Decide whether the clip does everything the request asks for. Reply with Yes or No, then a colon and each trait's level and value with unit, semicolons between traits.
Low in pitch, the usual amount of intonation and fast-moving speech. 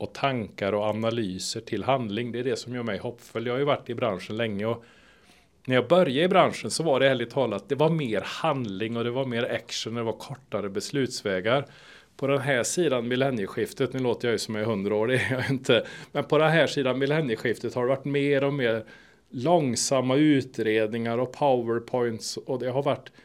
Yes: low, 125 Hz; average, 3.2 semitones; fast, 210 wpm